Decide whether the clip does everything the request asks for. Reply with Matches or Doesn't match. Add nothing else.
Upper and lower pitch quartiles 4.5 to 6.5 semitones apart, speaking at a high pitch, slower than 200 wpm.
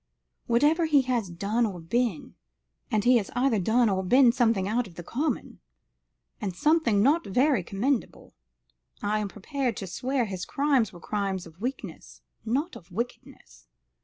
Matches